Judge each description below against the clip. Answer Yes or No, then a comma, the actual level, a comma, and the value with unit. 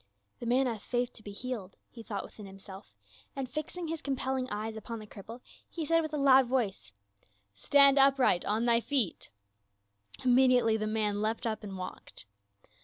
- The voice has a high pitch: Yes, high, 230 Hz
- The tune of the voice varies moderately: Yes, average, 4.5 semitones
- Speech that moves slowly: No, average, 180 wpm